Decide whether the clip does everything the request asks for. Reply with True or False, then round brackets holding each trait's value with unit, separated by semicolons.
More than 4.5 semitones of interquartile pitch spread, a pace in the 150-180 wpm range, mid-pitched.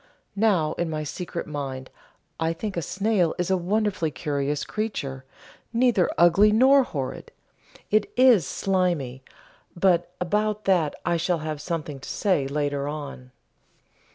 False (5.3 semitones; 135 wpm; 170 Hz)